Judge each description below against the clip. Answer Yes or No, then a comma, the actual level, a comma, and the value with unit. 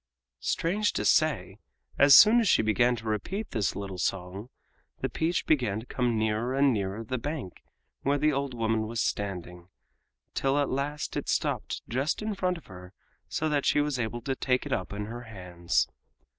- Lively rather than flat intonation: Yes, wide, 6.0 semitones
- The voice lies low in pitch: Yes, low, 120 Hz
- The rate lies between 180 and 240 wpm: Yes, average, 185 wpm